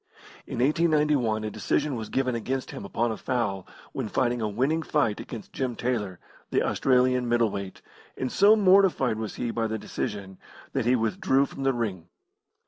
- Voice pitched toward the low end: Yes, low, 120 Hz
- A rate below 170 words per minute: No, average, 175 wpm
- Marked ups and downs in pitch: No, average, 3.6 semitones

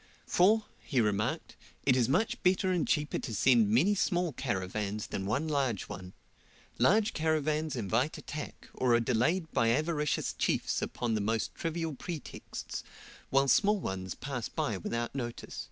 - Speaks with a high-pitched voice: No, low, 135 Hz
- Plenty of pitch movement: Yes, wide, 6.3 semitones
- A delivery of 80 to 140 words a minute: No, average, 155 wpm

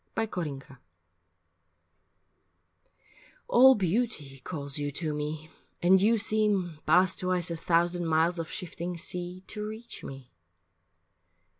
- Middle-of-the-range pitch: Yes, medium, 175 Hz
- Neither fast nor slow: No, slow, 125 wpm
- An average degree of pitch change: Yes, average, 3.6 semitones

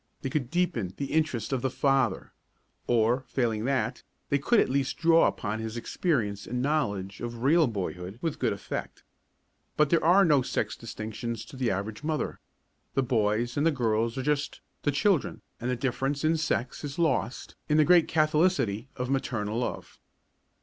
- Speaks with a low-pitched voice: Yes, low, 130 Hz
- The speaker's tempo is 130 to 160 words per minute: No, average, 175 wpm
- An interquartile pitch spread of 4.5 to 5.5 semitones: Yes, average, 5.0 semitones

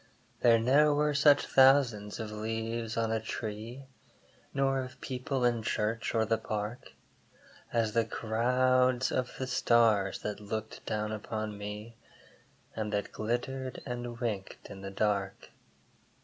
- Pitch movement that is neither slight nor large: Yes, average, 3.0 semitones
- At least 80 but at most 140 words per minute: Yes, slow, 135 wpm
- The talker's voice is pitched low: Yes, low, 115 Hz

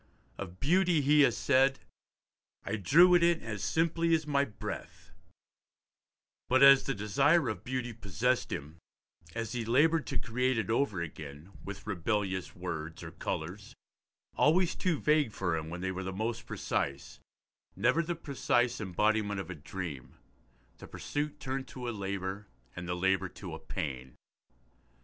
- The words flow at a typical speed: Yes, average, 155 wpm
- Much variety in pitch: Yes, wide, 6.9 semitones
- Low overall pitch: Yes, low, 110 Hz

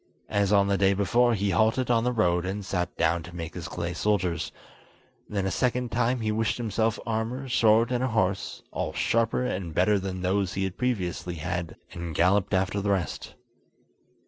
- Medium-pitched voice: No, low, 100 Hz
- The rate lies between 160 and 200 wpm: Yes, average, 190 wpm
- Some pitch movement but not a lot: Yes, average, 3.9 semitones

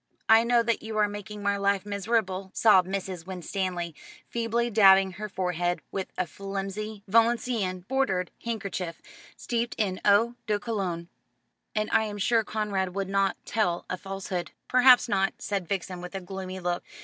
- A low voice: No, high, 200 Hz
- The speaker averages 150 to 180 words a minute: Yes, average, 160 wpm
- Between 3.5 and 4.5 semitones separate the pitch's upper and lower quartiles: No, average, 2.8 semitones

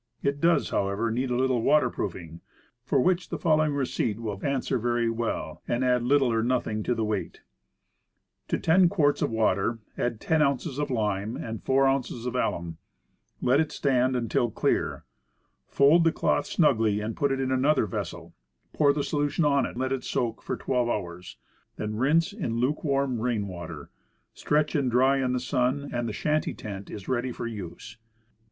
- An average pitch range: Yes, average, 3.9 semitones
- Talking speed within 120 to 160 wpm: No, average, 185 wpm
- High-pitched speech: No, low, 125 Hz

